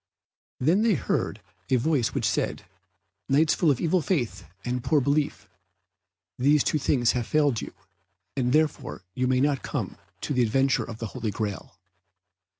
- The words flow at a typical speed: Yes, average, 160 wpm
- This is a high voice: No, low, 135 Hz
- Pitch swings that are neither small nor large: Yes, average, 3.9 semitones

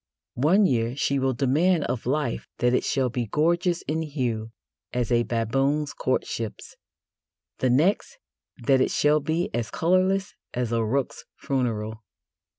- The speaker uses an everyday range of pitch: Yes, average, 4.6 semitones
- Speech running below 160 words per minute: Yes, average, 145 wpm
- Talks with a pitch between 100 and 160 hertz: Yes, low, 135 Hz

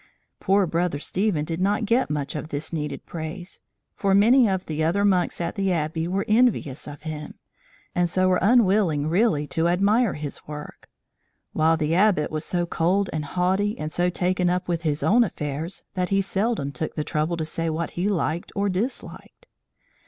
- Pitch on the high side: No, medium, 175 Hz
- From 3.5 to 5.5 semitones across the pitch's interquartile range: Yes, average, 4.0 semitones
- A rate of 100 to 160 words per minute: No, average, 185 wpm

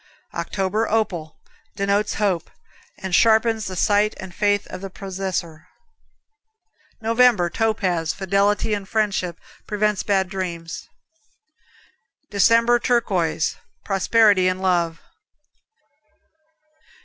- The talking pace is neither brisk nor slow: No, slow, 90 wpm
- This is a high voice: Yes, high, 195 Hz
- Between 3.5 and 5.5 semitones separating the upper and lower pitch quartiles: No, narrow, 2.6 semitones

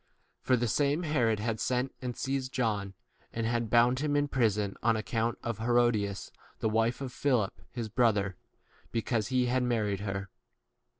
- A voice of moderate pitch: No, low, 115 Hz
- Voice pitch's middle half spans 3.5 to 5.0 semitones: No, average, 2.8 semitones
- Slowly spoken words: No, average, 175 wpm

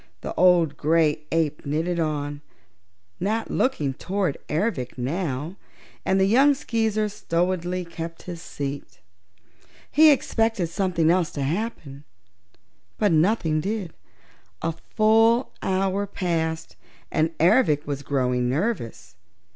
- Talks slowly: Yes, slow, 115 wpm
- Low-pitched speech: No, medium, 170 Hz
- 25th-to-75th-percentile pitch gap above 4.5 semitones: Yes, average, 5.1 semitones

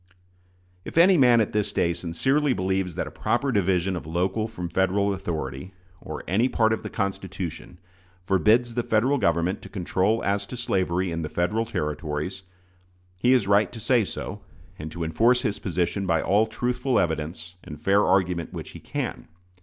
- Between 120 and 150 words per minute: No, average, 175 wpm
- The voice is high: No, very low, 95 Hz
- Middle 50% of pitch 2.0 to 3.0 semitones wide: No, average, 4.6 semitones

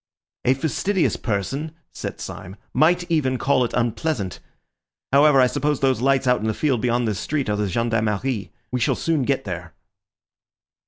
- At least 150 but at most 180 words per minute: Yes, average, 165 wpm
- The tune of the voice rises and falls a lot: No, average, 4.8 semitones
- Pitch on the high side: No, low, 125 Hz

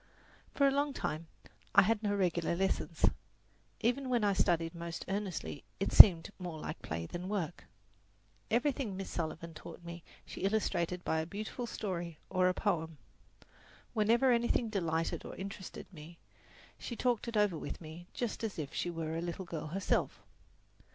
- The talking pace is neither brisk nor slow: Yes, average, 165 wpm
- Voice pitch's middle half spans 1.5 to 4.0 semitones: No, average, 4.5 semitones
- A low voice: No, medium, 185 Hz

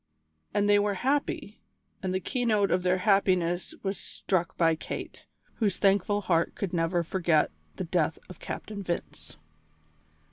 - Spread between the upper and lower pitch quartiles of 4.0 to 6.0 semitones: No, average, 2.8 semitones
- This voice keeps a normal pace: Yes, average, 145 wpm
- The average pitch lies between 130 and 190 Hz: Yes, medium, 185 Hz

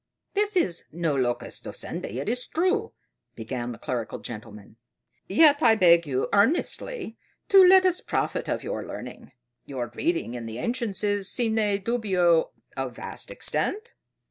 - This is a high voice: Yes, high, 200 Hz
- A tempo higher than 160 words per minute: No, average, 145 wpm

